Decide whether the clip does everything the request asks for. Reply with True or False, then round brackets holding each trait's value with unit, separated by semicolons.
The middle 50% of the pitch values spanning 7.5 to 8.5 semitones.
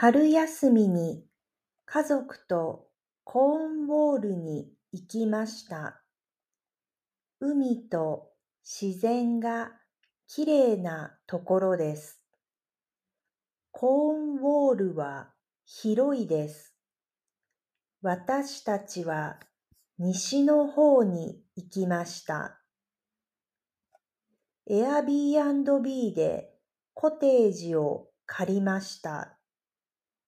True (7.9 semitones)